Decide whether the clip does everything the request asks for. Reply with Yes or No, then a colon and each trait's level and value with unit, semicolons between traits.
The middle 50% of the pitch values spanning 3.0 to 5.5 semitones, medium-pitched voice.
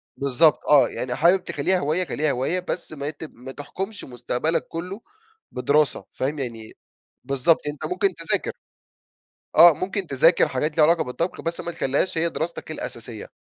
Yes: average, 4.3 semitones; medium, 155 Hz